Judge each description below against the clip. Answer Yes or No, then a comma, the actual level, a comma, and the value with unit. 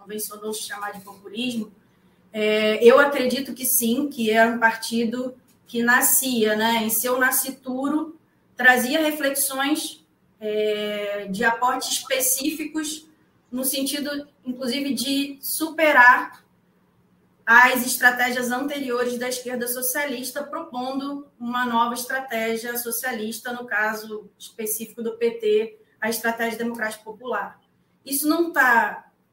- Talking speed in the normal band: No, slow, 110 wpm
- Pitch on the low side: No, very high, 250 Hz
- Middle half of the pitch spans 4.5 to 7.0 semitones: No, average, 3.1 semitones